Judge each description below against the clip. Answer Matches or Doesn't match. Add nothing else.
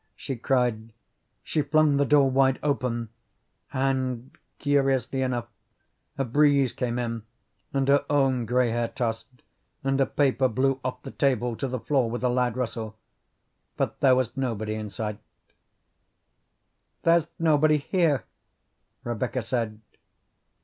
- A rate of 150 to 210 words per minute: Doesn't match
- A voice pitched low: Matches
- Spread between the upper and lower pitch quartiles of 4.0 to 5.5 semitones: Doesn't match